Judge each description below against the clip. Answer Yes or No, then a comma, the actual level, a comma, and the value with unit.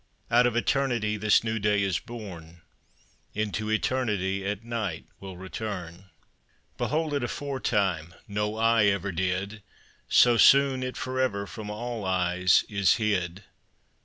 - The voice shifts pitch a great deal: No, average, 3.8 semitones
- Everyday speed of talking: No, slow, 130 wpm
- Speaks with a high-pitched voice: No, low, 105 Hz